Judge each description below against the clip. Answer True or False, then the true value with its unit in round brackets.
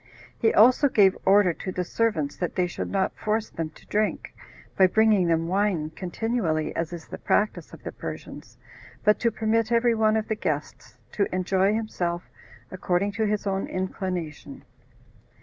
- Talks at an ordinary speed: True (165 wpm)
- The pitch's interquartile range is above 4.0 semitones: False (3.6 semitones)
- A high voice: True (195 Hz)